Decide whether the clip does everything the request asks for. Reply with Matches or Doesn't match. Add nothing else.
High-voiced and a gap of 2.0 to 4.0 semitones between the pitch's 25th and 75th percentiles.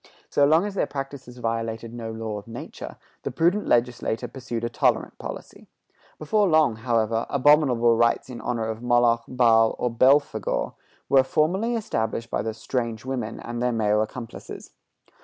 Doesn't match